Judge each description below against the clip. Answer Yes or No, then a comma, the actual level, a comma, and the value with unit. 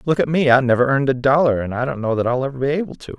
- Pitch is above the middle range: No, low, 135 Hz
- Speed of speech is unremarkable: No, fast, 340 wpm